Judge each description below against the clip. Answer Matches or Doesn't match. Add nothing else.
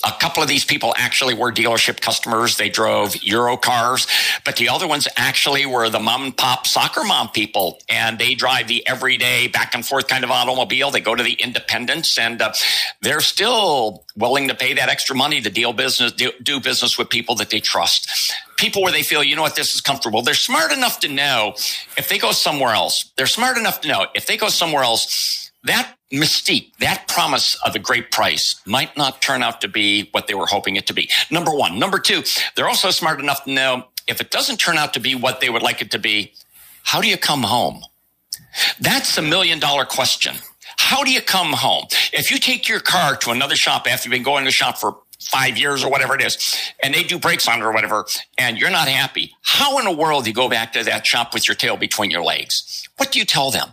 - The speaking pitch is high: Doesn't match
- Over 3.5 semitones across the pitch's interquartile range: Matches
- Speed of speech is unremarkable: Doesn't match